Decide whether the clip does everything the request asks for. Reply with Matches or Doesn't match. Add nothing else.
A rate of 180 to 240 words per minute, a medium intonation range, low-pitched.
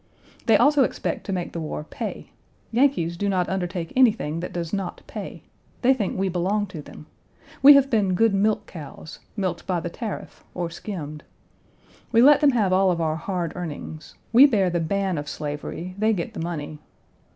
Doesn't match